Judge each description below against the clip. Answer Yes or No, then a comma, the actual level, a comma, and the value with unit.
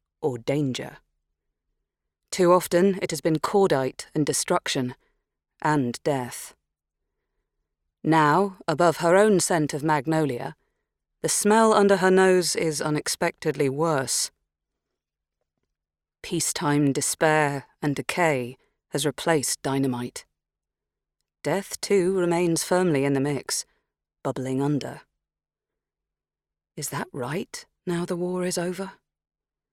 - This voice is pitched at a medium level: Yes, medium, 160 Hz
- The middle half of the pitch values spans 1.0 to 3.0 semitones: No, average, 4.2 semitones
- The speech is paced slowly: Yes, slow, 105 wpm